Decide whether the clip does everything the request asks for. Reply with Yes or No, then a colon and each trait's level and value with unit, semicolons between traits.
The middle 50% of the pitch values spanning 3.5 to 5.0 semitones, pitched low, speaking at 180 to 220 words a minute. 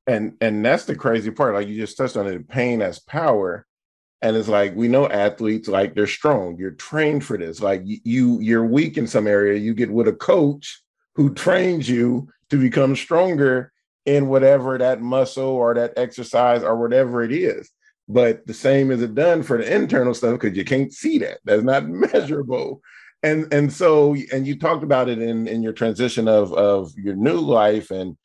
Yes: average, 4.5 semitones; low, 120 Hz; average, 200 wpm